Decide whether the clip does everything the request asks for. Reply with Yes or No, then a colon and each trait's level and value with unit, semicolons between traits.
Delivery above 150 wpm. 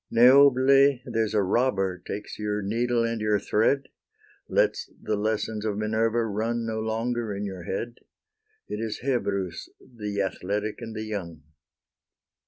No: average, 140 wpm